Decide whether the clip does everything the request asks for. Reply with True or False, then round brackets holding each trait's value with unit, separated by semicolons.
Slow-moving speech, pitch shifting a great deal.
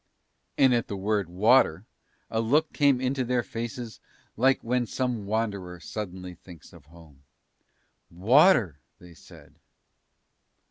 True (125 wpm; 5.9 semitones)